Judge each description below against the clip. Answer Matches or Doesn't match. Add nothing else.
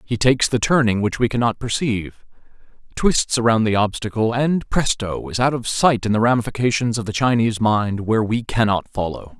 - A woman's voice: Doesn't match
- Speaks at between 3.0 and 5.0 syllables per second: Doesn't match